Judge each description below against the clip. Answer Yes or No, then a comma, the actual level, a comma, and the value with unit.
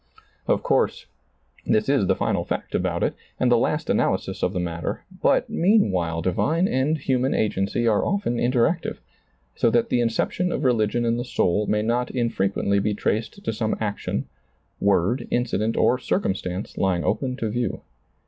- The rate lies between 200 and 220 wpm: No, average, 165 wpm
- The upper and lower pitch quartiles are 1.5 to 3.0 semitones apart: No, average, 4.2 semitones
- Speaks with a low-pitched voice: Yes, low, 115 Hz